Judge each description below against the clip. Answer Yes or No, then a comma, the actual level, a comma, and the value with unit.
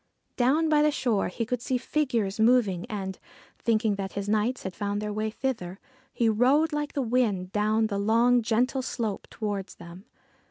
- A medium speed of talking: Yes, average, 175 wpm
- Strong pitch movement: No, average, 3.8 semitones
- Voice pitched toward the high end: Yes, high, 220 Hz